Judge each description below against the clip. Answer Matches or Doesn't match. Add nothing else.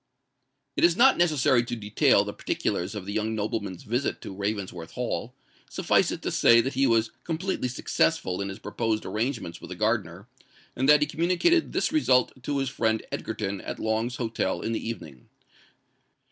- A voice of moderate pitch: Doesn't match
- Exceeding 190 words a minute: Doesn't match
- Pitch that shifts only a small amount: Doesn't match